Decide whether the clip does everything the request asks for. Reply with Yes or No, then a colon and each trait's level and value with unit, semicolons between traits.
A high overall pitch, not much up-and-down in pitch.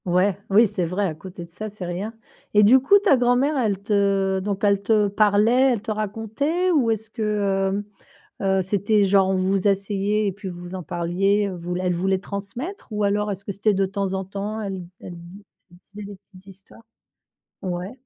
Yes: high, 200 Hz; narrow, 2.0 semitones